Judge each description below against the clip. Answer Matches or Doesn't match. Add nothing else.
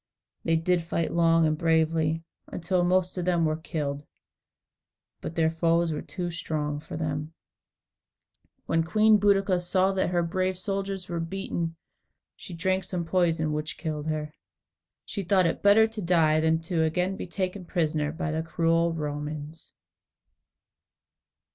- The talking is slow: Doesn't match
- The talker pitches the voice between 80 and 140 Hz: Doesn't match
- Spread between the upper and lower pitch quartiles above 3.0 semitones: Doesn't match